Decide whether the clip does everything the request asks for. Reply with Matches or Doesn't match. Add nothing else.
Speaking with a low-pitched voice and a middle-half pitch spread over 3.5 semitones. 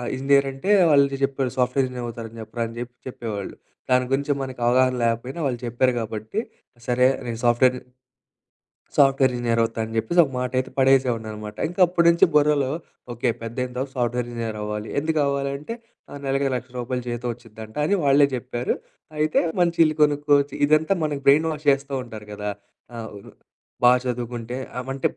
Doesn't match